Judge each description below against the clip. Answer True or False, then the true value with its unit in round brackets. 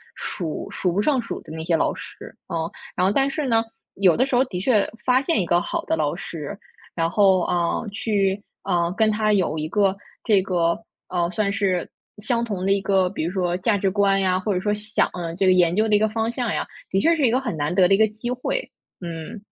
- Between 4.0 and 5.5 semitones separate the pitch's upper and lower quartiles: False (3.6 semitones)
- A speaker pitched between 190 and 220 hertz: True (195 Hz)